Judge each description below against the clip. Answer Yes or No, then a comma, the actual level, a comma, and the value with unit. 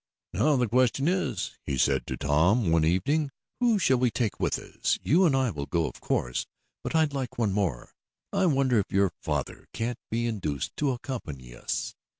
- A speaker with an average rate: Yes, average, 190 wpm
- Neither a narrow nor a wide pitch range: No, wide, 8.0 semitones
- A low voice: Yes, low, 120 Hz